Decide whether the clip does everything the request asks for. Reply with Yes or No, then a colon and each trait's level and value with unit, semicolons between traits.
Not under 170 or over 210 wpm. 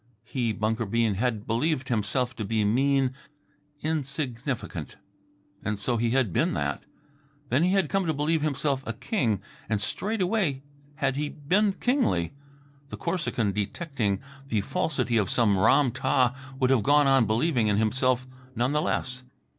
No: average, 155 wpm